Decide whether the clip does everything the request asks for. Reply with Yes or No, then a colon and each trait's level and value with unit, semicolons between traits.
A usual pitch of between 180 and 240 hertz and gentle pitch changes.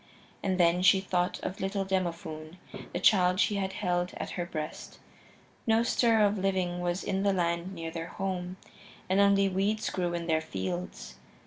Yes: medium, 185 Hz; narrow, 2.1 semitones